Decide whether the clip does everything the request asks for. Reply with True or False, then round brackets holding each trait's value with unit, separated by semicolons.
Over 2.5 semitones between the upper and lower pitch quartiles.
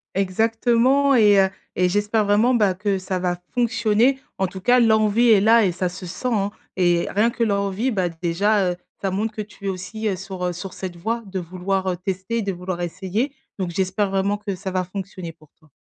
True (2.9 semitones)